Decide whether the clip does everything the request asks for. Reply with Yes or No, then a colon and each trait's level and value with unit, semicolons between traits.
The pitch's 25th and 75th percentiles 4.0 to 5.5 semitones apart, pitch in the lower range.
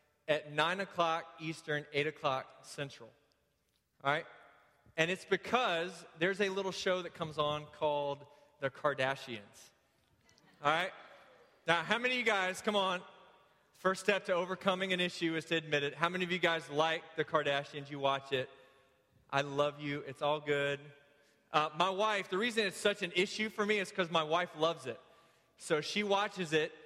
No: average, 4.3 semitones; medium, 165 Hz